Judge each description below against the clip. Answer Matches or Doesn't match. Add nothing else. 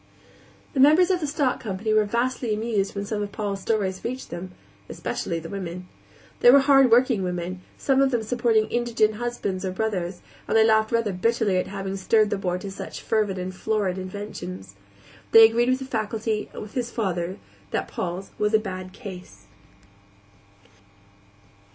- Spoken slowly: Doesn't match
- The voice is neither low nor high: Doesn't match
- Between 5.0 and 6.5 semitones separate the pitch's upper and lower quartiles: Doesn't match